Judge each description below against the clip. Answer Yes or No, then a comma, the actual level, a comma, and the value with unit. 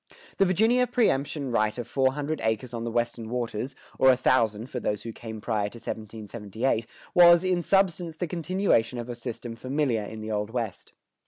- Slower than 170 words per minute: No, average, 185 wpm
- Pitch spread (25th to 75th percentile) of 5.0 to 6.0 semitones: Yes, wide, 5.6 semitones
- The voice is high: No, low, 120 Hz